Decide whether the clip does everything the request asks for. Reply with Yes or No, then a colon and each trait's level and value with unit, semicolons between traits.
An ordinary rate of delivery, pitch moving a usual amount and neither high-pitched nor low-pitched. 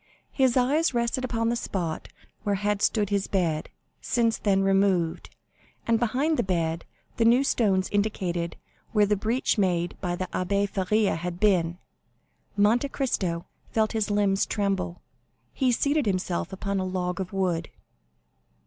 No: average, 150 wpm; average, 3.8 semitones; high, 200 Hz